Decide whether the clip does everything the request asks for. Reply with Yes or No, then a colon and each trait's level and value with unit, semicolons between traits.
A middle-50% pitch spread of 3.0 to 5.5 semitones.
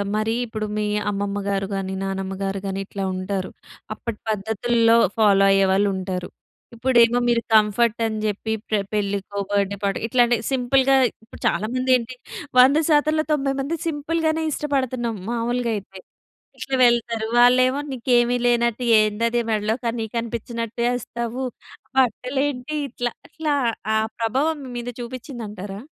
Yes: average, 3.5 semitones